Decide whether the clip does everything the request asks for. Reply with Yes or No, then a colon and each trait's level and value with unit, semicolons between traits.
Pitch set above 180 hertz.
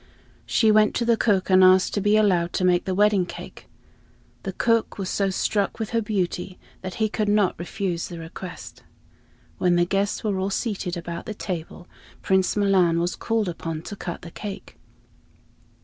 Yes: high, 190 Hz